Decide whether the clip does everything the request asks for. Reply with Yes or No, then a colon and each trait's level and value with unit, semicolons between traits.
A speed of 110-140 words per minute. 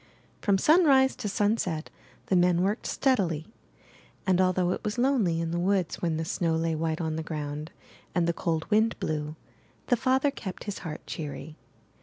No: average, 175 wpm